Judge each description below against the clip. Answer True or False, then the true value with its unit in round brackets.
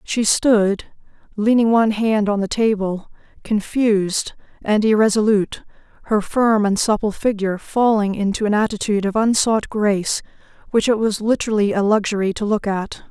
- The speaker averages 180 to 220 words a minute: False (145 wpm)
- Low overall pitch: False (210 Hz)